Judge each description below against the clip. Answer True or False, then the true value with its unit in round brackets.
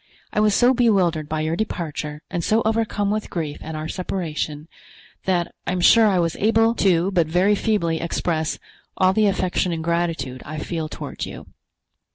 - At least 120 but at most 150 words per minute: False (180 wpm)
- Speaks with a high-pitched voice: False (175 Hz)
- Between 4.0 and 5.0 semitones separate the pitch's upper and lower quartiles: True (4.3 semitones)